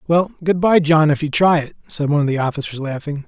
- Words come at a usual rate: No, fast, 255 wpm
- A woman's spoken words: No, male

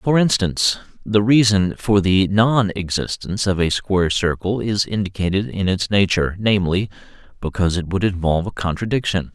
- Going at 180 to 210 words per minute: No, average, 150 wpm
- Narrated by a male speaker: Yes, male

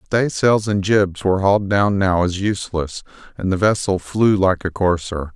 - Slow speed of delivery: No, average, 190 wpm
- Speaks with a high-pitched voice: No, very low, 95 Hz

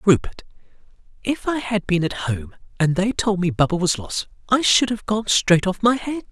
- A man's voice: Yes, male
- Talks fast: Yes, fast, 210 wpm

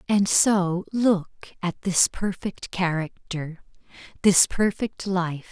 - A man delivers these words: No, female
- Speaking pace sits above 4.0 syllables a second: No, 3.3 syllables/s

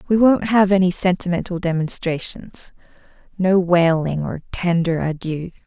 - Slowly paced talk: Yes, slow, 115 wpm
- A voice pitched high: No, medium, 175 Hz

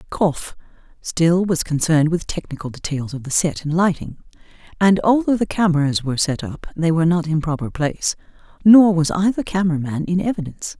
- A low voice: No, medium, 170 Hz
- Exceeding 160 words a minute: Yes, average, 180 wpm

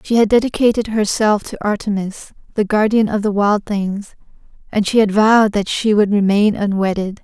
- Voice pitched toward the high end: Yes, high, 210 Hz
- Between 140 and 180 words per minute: Yes, average, 175 wpm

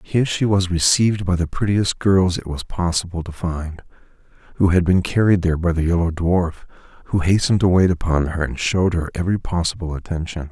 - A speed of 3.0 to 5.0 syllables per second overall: No, 5.9 syllables/s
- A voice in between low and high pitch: No, very low, 90 Hz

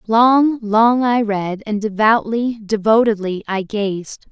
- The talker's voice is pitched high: Yes, high, 215 Hz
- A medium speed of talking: No, slow, 95 wpm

